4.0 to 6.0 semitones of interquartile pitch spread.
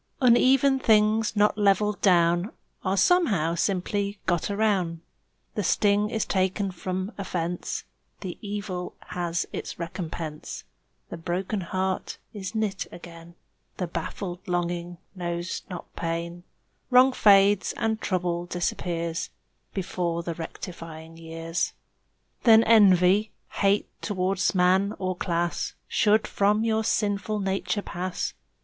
No: average, 3.2 semitones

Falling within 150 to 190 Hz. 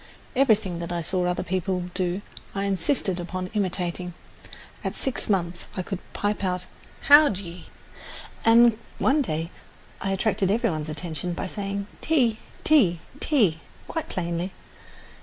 Yes: medium, 185 Hz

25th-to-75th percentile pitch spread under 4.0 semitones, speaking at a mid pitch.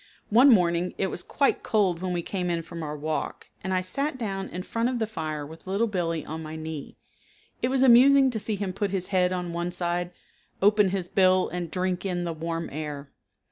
Yes: average, 3.6 semitones; medium, 180 Hz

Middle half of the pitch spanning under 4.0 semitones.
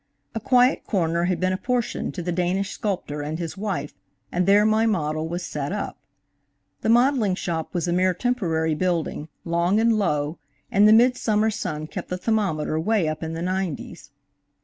No: average, 4.8 semitones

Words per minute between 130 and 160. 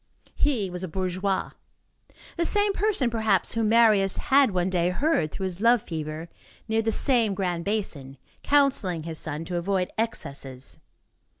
Yes: average, 155 wpm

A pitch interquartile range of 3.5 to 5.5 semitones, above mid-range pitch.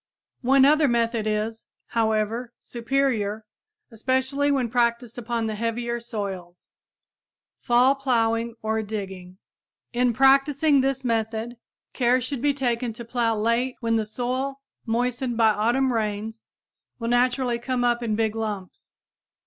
No: narrow, 2.5 semitones; high, 235 Hz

